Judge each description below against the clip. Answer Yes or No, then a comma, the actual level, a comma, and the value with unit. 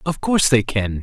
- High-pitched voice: No, low, 125 Hz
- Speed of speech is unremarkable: No, fast, 235 wpm